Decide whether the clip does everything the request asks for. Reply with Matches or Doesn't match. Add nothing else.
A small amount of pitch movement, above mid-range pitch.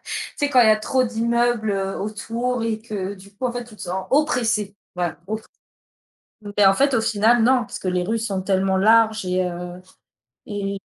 Doesn't match